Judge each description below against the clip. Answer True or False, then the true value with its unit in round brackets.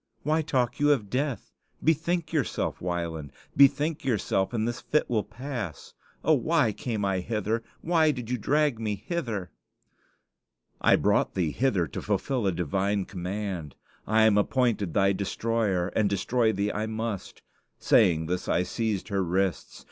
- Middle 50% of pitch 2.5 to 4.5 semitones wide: False (4.9 semitones)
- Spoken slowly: False (155 wpm)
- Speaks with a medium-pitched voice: False (110 Hz)